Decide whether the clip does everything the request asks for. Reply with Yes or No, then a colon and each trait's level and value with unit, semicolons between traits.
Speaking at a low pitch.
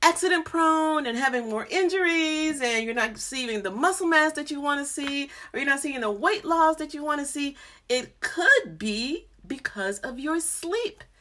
No: very high, 305 Hz